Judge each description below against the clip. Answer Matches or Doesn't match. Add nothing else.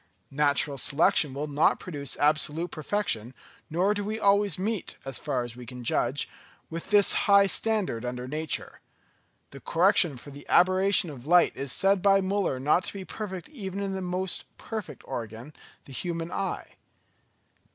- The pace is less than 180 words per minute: Matches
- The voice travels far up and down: Matches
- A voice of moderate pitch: Matches